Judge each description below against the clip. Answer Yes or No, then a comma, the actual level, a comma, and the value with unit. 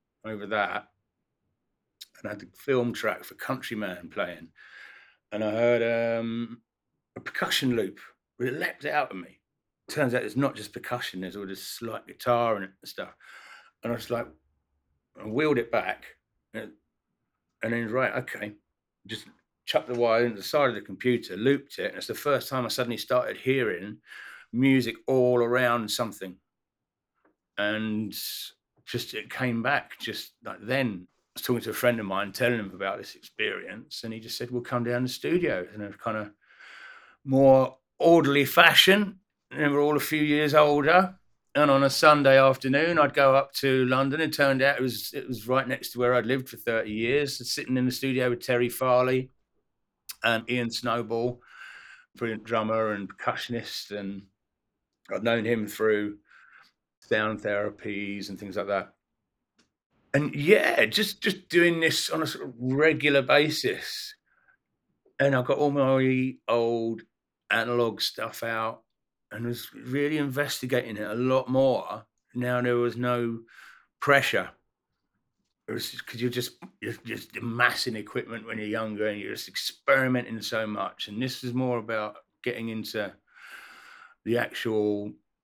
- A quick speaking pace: No, average, 165 wpm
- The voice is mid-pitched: No, low, 120 Hz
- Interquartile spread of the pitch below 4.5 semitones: Yes, average, 3.4 semitones